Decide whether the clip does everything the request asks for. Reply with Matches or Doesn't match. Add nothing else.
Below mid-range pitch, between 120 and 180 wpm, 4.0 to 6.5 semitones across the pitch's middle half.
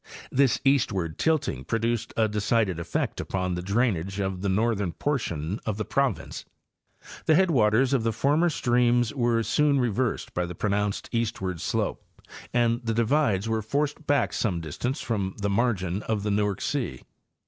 Matches